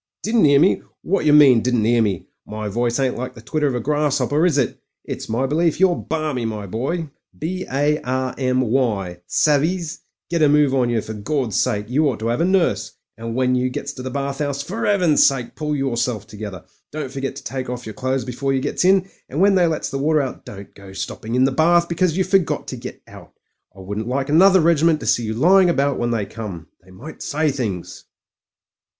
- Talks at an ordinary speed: No, fast, 225 wpm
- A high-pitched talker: No, low, 135 Hz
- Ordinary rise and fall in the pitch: Yes, average, 4.9 semitones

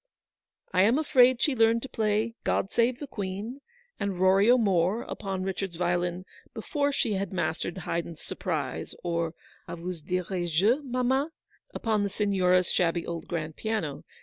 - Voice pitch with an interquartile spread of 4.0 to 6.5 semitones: Yes, average, 4.7 semitones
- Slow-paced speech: No, average, 160 wpm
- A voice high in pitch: Yes, high, 195 Hz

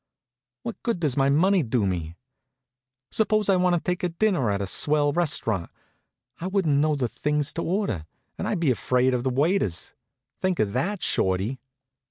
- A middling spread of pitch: No, wide, 6.8 semitones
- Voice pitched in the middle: Yes, medium, 150 Hz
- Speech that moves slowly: No, average, 175 wpm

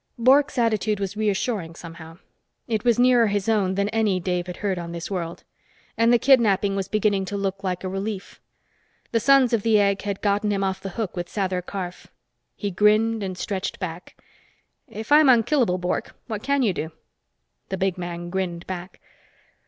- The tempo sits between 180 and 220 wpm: Yes, average, 185 wpm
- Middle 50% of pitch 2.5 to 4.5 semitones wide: Yes, average, 3.3 semitones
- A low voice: No, high, 200 Hz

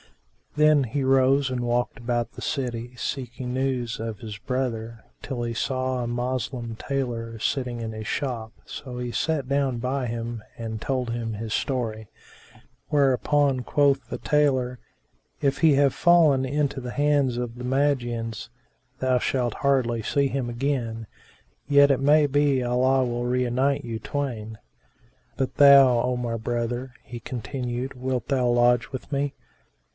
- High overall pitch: No, low, 125 Hz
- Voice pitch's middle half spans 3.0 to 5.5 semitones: No, narrow, 2.5 semitones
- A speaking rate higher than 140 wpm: Yes, average, 150 wpm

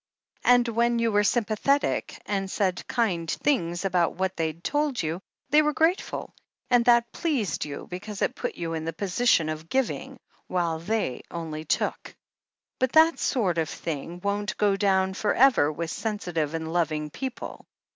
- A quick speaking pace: No, average, 165 wpm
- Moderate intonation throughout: No, wide, 6.2 semitones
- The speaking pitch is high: Yes, high, 195 Hz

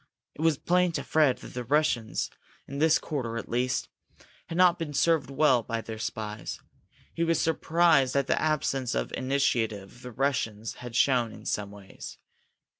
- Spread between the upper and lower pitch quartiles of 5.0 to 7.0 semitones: Yes, average, 5.3 semitones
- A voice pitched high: No, low, 135 Hz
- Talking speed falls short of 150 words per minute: No, average, 170 wpm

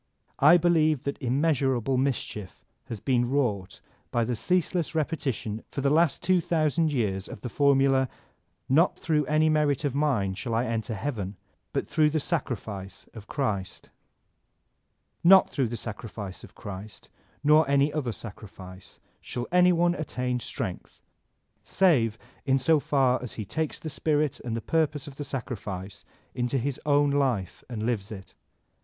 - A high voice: No, low, 135 Hz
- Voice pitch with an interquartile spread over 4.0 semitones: Yes, average, 5.3 semitones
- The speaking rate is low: No, average, 155 wpm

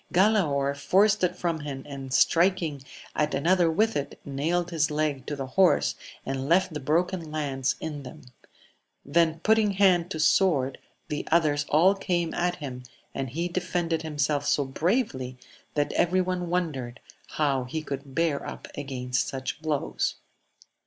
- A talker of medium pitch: Yes, medium, 155 Hz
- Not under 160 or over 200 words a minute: No, average, 150 wpm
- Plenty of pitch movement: No, average, 4.1 semitones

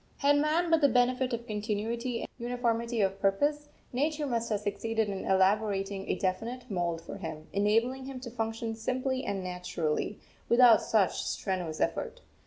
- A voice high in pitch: Yes, high, 225 Hz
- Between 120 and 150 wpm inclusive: No, average, 160 wpm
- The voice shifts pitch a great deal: No, average, 4.4 semitones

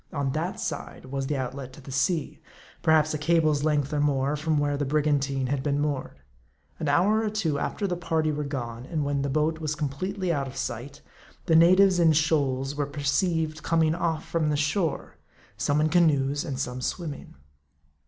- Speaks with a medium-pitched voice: Yes, medium, 150 Hz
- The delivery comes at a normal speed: Yes, average, 190 wpm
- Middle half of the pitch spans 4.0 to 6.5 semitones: No, narrow, 2.6 semitones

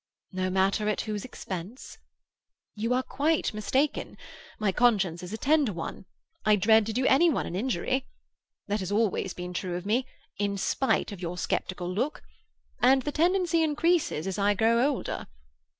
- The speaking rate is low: No, average, 165 wpm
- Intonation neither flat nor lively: No, wide, 5.8 semitones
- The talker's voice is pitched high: Yes, high, 215 Hz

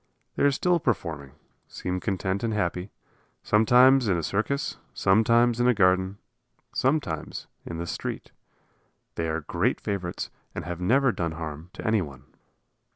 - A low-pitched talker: Yes, very low, 95 Hz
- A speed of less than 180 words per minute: Yes, average, 145 wpm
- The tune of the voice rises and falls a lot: Yes, wide, 5.9 semitones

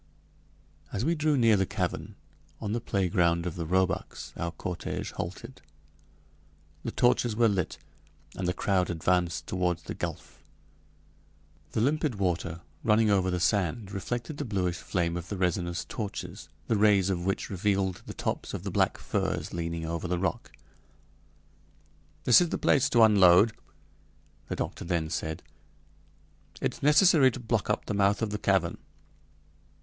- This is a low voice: Yes, very low, 95 Hz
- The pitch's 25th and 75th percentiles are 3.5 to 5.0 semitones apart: Yes, average, 4.3 semitones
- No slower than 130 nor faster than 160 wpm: Yes, average, 155 wpm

